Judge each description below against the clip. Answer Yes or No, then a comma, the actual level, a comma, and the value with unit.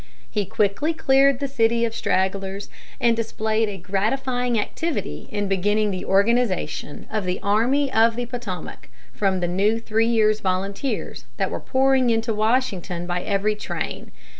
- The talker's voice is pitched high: Yes, high, 215 Hz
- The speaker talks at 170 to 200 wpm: No, average, 150 wpm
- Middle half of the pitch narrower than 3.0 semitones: No, average, 3.5 semitones